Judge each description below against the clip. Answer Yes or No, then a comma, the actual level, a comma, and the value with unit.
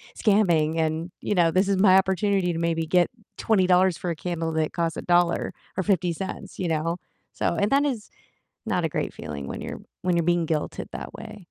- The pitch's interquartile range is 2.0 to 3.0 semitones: Yes, average, 2.7 semitones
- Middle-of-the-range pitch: Yes, medium, 175 Hz